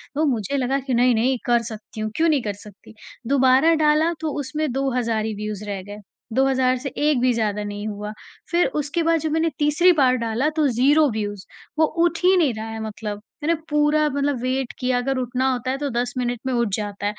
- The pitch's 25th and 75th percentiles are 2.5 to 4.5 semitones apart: No, average, 5.0 semitones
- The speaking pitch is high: Yes, very high, 255 Hz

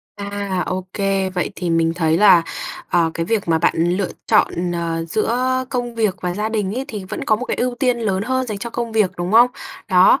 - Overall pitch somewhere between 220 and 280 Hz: No, high, 200 Hz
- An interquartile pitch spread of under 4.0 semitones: No, average, 4.3 semitones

